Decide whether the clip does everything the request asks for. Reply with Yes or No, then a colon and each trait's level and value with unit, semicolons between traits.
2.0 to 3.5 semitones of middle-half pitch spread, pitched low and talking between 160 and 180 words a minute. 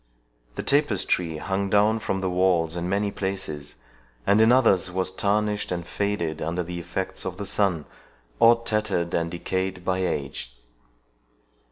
No: average, 2.9 semitones; very low, 95 Hz; average, 150 wpm